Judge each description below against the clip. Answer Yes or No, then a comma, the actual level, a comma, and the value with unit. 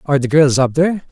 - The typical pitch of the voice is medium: Yes, medium, 145 Hz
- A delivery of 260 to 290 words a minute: Yes, fast, 270 wpm